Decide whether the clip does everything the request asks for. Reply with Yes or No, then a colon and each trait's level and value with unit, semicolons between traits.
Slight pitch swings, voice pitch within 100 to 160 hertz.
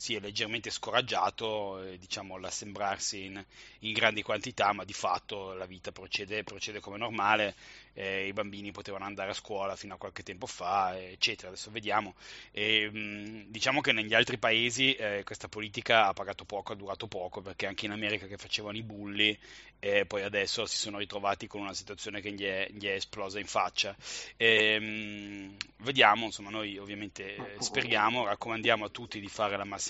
Yes: narrow, 1.7 semitones; low, 105 Hz